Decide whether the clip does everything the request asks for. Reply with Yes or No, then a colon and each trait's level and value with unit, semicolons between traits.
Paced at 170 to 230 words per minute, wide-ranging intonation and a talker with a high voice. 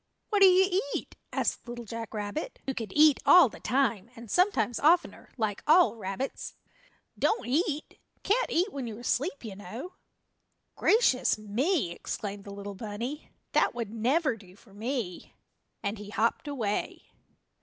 No: average, 155 wpm; wide, 6.9 semitones; high, 240 Hz